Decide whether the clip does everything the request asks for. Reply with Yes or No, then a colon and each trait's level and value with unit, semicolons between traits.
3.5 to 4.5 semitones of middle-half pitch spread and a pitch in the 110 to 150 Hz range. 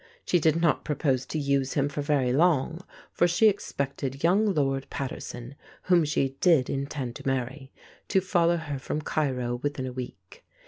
Yes: average, 3.8 semitones; medium, 140 Hz